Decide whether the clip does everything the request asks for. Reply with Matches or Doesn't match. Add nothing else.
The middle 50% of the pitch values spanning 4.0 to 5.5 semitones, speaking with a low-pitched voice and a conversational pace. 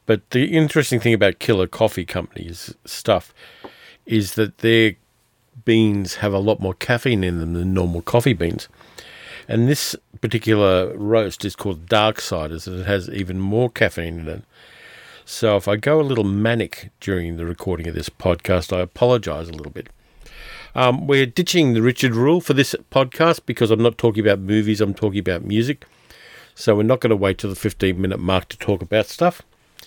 Matches